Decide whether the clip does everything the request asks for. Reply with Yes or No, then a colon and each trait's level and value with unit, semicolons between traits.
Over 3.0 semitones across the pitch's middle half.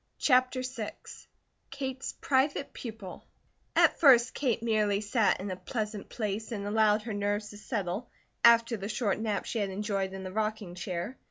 No: average, 2.7 semitones